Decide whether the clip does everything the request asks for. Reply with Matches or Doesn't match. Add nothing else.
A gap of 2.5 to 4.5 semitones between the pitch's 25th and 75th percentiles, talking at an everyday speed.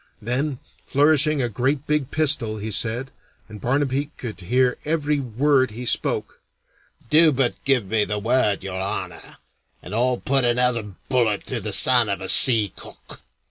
Matches